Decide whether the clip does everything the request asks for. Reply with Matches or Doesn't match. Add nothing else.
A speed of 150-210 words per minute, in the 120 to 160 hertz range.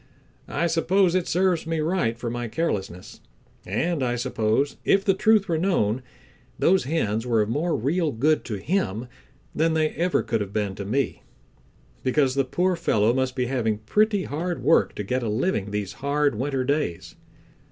Matches